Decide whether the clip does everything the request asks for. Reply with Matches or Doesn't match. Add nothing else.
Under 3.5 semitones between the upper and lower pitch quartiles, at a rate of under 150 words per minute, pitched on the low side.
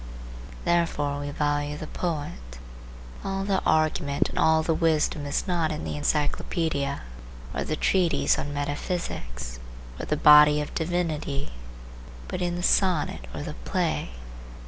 Doesn't match